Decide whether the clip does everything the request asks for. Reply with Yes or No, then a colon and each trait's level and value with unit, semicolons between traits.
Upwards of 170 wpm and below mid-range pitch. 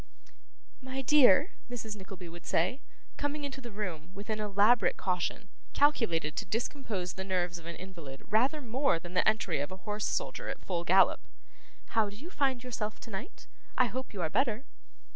No: average, 180 wpm; high, 210 Hz